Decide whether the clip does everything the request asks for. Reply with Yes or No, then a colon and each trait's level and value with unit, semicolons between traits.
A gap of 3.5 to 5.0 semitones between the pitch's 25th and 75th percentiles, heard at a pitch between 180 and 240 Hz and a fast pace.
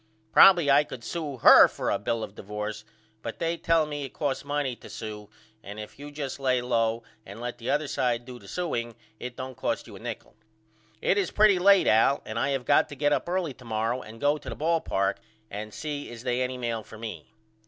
No: average, 4.4 semitones; low, 125 Hz; fast, 230 wpm